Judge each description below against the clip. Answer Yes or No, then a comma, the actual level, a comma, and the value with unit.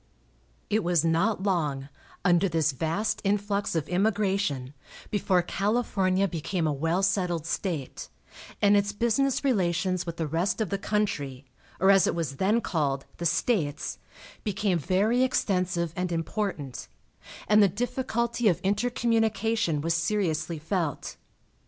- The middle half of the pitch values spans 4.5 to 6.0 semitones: No, average, 4.1 semitones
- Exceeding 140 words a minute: No, slow, 135 wpm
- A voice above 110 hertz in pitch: Yes, medium, 185 Hz